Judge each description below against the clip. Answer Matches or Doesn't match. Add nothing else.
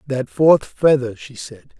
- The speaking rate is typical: Matches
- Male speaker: Matches